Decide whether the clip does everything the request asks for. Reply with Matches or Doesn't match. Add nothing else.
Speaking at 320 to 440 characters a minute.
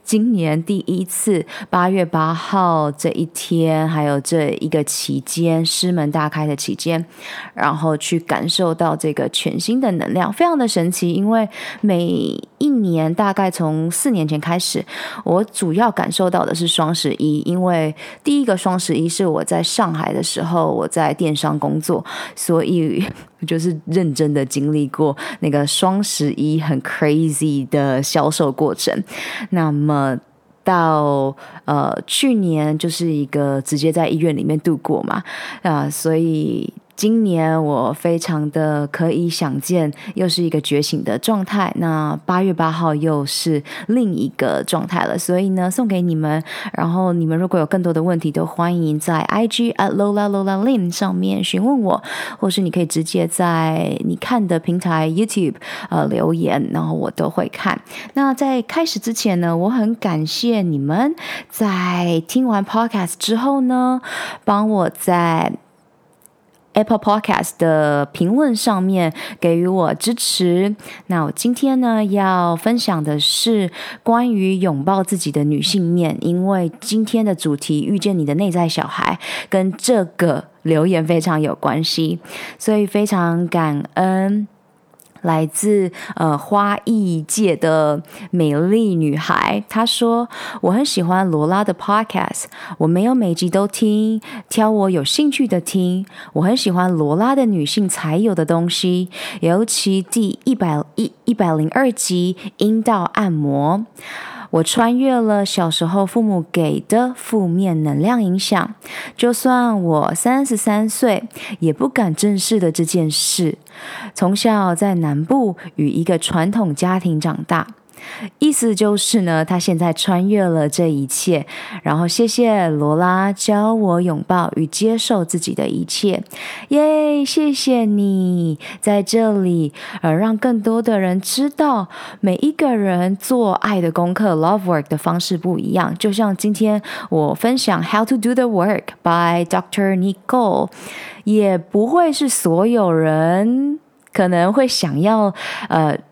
Doesn't match